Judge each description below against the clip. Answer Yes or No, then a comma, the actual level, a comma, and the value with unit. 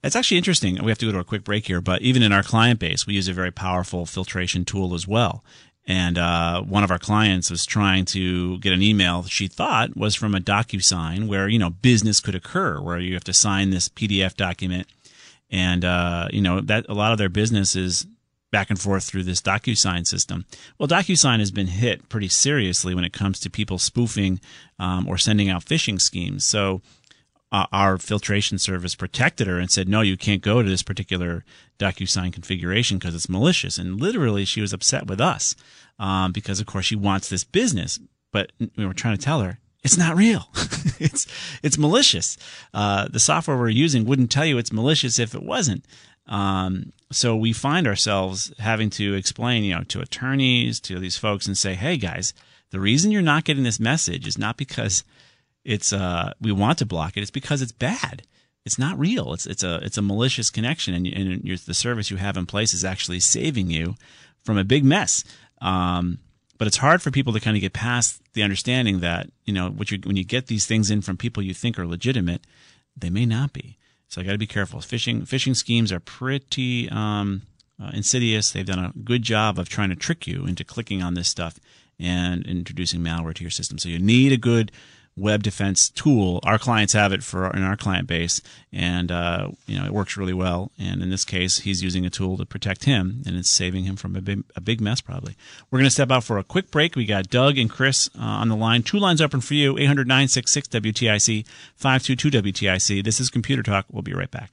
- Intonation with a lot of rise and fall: No, average, 4.6 semitones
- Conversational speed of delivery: No, fast, 220 wpm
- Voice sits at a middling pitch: No, low, 100 Hz